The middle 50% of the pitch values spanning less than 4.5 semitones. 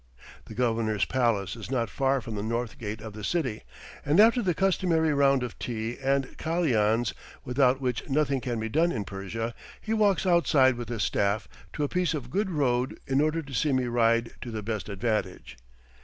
No: average, 4.9 semitones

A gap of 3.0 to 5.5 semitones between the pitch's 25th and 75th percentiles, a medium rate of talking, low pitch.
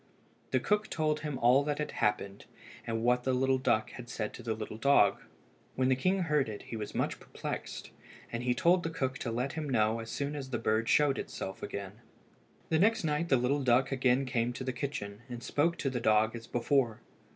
No: average, 4.1 semitones; fast, 215 wpm; low, 125 Hz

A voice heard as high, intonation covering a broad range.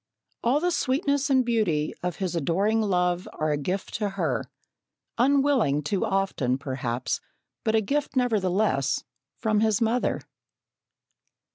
Yes: high, 200 Hz; wide, 6.8 semitones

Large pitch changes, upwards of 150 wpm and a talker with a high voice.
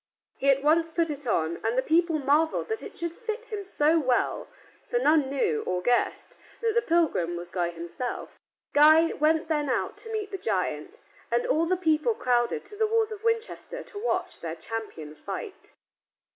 Yes: wide, 8.7 semitones; average, 185 wpm; very high, 315 Hz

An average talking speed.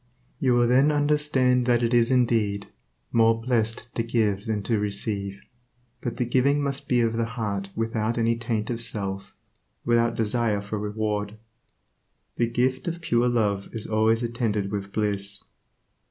Yes: average, 155 wpm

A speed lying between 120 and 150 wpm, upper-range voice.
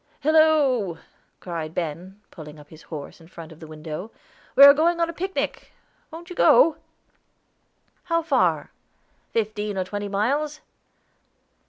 Yes: average, 140 wpm; high, 205 Hz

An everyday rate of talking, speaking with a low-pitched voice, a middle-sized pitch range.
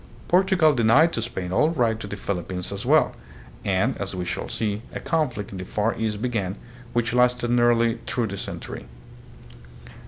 Yes: average, 175 wpm; low, 115 Hz; average, 3.7 semitones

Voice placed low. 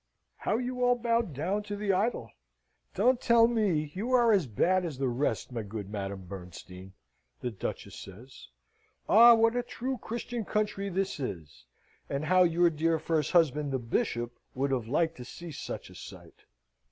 No: medium, 165 Hz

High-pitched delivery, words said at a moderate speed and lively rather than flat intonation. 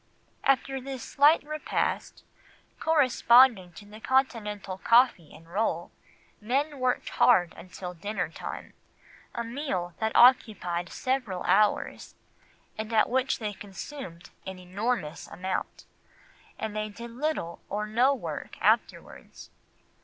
No: high, 220 Hz; slow, 115 wpm; wide, 5.7 semitones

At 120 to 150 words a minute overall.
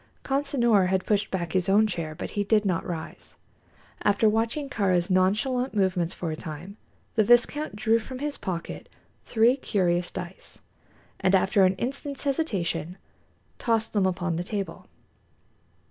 Yes: average, 145 wpm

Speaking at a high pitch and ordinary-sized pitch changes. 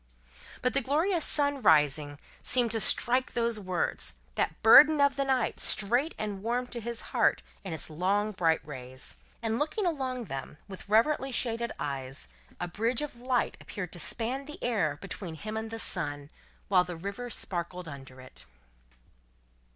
No: high, 220 Hz; wide, 6.8 semitones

